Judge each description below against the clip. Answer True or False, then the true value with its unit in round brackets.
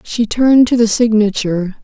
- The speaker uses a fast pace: False (165 wpm)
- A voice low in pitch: False (220 Hz)